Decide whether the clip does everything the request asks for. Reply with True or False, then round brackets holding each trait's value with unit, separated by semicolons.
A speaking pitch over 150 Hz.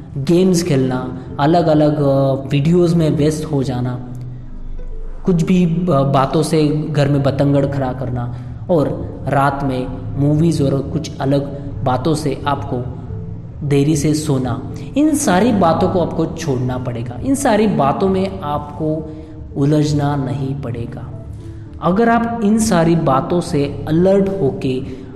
False (140 Hz)